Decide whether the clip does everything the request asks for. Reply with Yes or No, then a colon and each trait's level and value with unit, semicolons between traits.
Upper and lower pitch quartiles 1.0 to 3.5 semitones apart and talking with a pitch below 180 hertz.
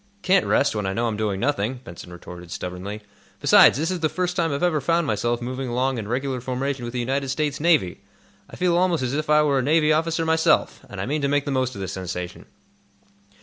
No: wide, 5.5 semitones; low, 135 Hz